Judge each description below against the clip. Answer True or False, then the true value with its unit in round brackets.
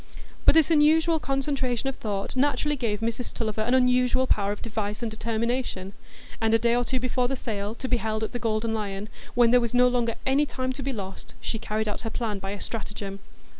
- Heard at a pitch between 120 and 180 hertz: False (235 Hz)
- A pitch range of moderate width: True (3.0 semitones)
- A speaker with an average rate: False (220 wpm)